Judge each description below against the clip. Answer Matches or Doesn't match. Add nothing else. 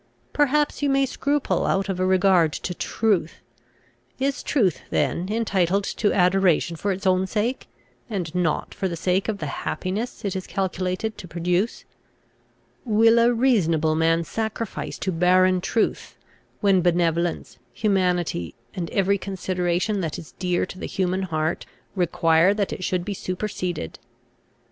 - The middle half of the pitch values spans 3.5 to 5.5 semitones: Doesn't match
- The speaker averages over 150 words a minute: Doesn't match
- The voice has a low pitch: Doesn't match